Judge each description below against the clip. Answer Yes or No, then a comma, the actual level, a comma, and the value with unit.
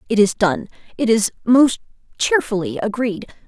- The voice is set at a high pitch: Yes, high, 220 Hz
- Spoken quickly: No, slow, 120 wpm